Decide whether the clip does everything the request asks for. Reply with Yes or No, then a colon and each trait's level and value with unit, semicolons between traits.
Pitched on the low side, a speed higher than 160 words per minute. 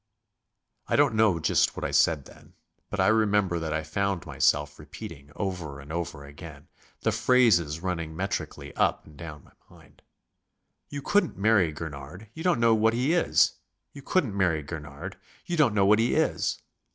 Yes: very low, 90 Hz; average, 175 wpm